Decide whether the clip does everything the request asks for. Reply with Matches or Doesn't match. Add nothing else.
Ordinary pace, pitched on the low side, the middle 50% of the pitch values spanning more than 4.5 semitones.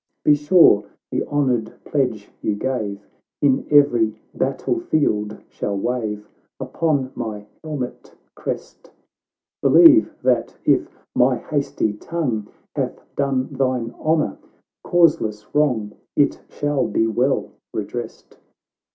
Doesn't match